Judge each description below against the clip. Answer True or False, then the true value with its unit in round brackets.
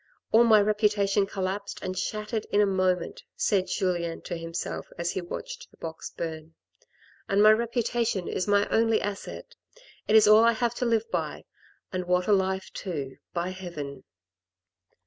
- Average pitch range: True (3.2 semitones)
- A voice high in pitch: True (195 Hz)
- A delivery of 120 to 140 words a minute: False (170 wpm)